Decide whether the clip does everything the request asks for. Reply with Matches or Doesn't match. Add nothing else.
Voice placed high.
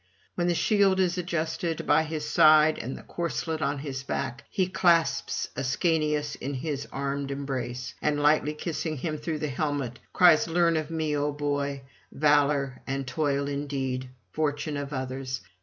Doesn't match